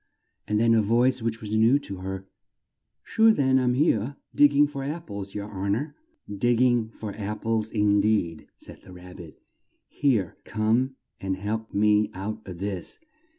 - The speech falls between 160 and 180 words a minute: Yes, average, 175 wpm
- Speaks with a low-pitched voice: Yes, low, 110 Hz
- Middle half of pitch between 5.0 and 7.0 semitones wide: No, average, 3.8 semitones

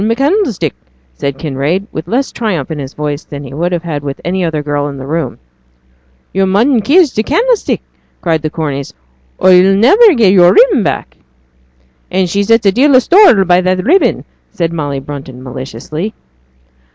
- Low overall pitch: No, medium, 180 Hz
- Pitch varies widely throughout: Yes, wide, 7.7 semitones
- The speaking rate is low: No, average, 185 wpm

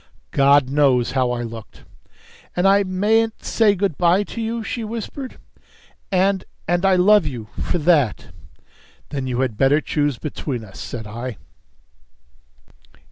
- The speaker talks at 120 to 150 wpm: Yes, average, 140 wpm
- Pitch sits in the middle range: Yes, medium, 150 Hz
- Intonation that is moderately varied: No, wide, 7.7 semitones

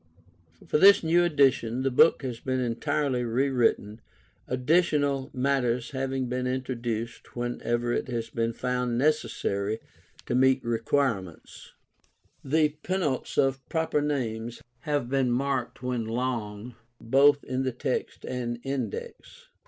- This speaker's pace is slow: Yes, slow, 125 wpm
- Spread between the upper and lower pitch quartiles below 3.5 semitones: Yes, average, 2.8 semitones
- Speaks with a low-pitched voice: Yes, low, 130 Hz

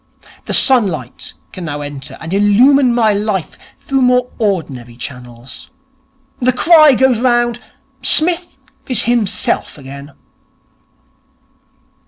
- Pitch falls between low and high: No, high, 220 Hz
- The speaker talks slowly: Yes, slow, 105 wpm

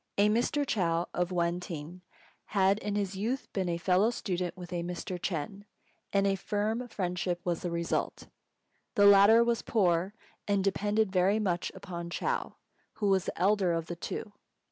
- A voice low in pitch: No, high, 190 Hz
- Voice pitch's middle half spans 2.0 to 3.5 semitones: Yes, average, 2.9 semitones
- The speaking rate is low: No, average, 165 wpm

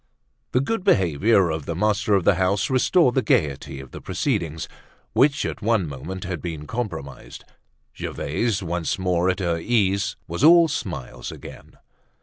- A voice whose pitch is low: Yes, very low, 95 Hz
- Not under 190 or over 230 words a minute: No, average, 155 wpm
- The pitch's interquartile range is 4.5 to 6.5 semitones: Yes, wide, 5.4 semitones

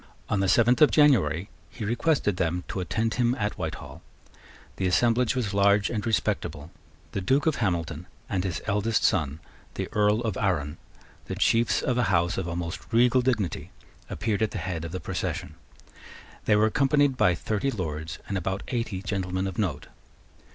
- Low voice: Yes, low, 100 Hz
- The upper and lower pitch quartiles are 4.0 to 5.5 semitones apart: Yes, average, 4.6 semitones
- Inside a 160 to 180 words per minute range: Yes, average, 170 wpm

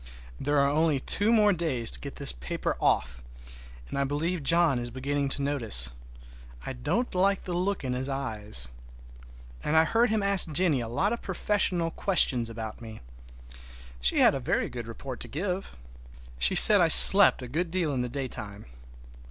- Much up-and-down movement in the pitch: Yes, wide, 7.1 semitones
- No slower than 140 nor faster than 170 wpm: No, average, 180 wpm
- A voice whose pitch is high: No, medium, 140 Hz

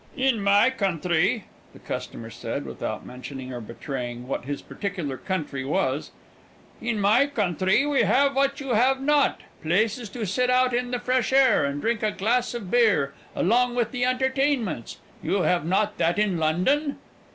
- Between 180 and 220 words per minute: No, average, 165 wpm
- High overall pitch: Yes, high, 215 Hz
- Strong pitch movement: Yes, wide, 7.4 semitones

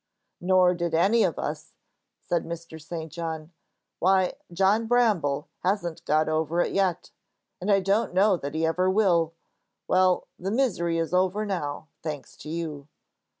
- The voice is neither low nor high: Yes, medium, 175 Hz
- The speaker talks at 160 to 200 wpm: No, average, 150 wpm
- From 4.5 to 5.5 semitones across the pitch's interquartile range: No, average, 3.0 semitones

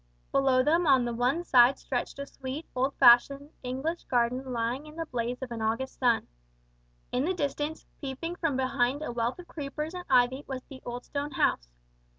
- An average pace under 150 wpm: No, average, 185 wpm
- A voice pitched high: Yes, very high, 265 Hz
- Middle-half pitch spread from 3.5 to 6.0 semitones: No, average, 3.1 semitones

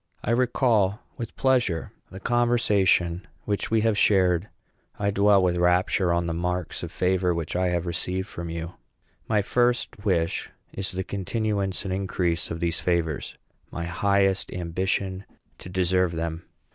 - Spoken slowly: No, average, 150 wpm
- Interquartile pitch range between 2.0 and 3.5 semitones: Yes, average, 2.8 semitones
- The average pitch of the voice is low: Yes, very low, 95 Hz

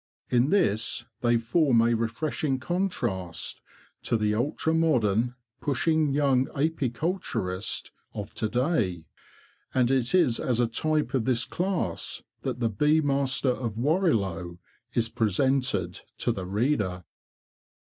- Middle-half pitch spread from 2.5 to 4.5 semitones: No, average, 5.3 semitones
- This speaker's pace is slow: Yes, slow, 125 wpm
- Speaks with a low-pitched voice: Yes, low, 125 Hz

